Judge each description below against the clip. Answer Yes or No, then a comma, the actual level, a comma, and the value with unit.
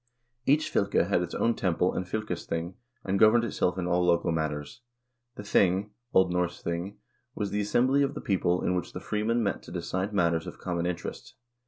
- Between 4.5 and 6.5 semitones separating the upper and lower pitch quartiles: No, average, 3.1 semitones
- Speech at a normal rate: Yes, average, 190 wpm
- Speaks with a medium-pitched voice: No, very low, 95 Hz